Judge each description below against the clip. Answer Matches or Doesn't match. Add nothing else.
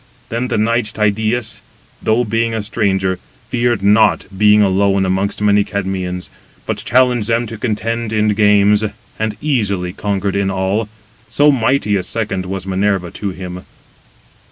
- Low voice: Matches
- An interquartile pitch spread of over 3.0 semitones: Doesn't match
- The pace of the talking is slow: Doesn't match